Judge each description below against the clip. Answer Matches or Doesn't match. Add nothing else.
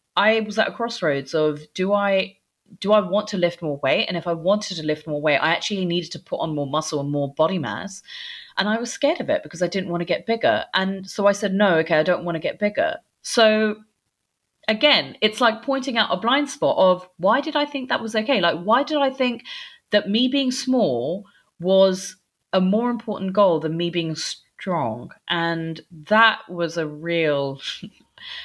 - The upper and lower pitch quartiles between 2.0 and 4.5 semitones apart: Doesn't match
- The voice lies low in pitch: Doesn't match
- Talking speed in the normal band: Doesn't match